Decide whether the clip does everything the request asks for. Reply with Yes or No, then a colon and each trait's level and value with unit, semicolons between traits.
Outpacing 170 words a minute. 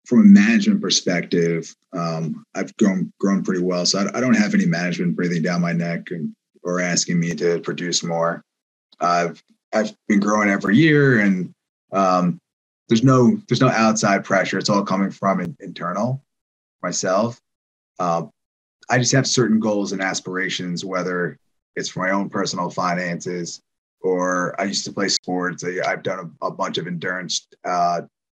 No: average, 165 wpm